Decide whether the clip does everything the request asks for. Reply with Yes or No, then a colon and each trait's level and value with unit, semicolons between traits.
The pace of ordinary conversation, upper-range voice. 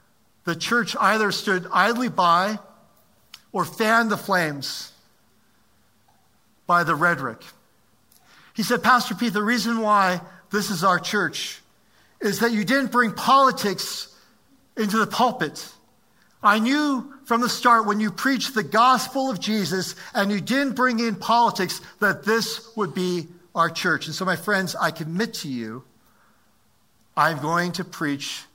Yes: average, 145 wpm; high, 205 Hz